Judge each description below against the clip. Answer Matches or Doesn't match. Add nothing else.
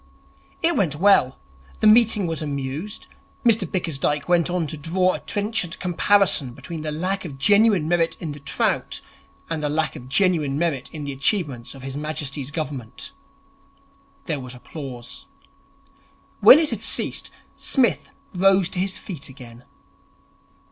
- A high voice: Doesn't match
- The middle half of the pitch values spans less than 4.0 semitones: Doesn't match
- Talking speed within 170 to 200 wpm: Doesn't match